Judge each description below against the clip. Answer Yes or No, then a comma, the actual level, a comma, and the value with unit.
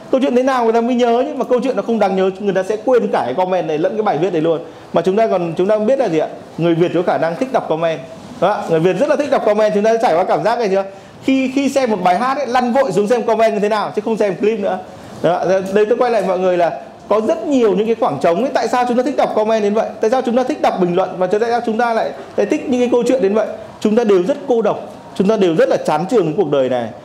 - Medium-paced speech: No, fast, 330 wpm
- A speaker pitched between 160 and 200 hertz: No, high, 220 Hz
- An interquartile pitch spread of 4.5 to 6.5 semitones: Yes, average, 4.9 semitones